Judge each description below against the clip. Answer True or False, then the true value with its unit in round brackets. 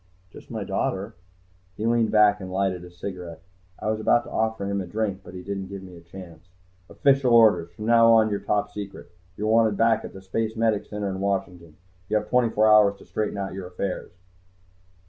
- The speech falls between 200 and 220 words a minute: True (205 wpm)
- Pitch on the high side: False (100 Hz)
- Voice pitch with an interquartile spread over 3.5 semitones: False (2.7 semitones)